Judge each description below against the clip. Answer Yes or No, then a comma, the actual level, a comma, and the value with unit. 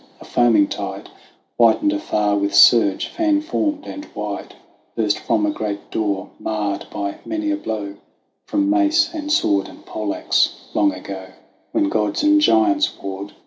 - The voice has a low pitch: Yes, low, 115 Hz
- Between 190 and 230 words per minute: No, average, 155 wpm